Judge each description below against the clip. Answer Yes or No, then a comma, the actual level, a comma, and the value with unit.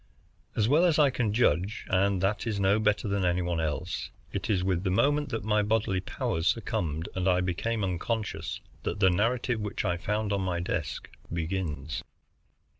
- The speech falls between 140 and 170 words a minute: No, average, 185 wpm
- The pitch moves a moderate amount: Yes, average, 3.6 semitones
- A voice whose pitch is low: Yes, very low, 95 Hz